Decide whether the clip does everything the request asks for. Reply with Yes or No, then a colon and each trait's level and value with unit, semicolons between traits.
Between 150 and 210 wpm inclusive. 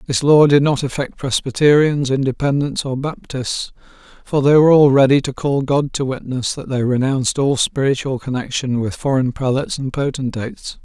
Yes: average, 165 wpm